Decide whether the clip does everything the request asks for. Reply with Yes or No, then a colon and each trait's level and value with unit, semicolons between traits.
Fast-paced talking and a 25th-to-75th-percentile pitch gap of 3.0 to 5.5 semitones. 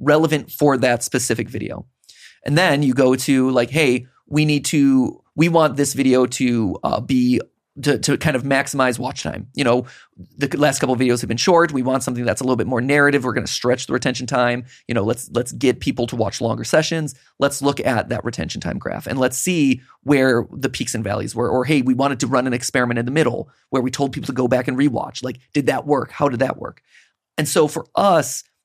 No: fast, 235 wpm; narrow, 2.4 semitones